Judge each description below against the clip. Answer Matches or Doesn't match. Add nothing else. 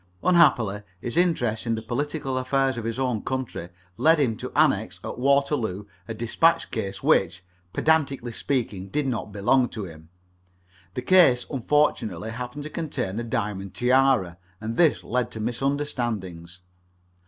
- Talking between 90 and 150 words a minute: Matches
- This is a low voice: Matches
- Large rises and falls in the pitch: Doesn't match